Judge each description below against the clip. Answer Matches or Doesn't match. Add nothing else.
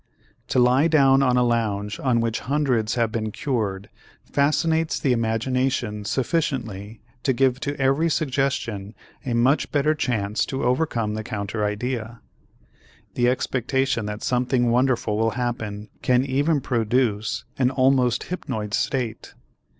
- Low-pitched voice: Matches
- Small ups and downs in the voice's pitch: Doesn't match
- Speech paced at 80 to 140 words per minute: Matches